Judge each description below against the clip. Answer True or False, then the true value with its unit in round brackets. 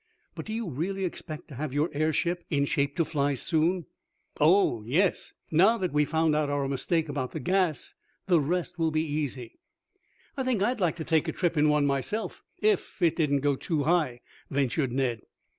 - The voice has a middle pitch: True (155 Hz)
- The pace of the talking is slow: False (195 wpm)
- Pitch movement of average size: True (3.7 semitones)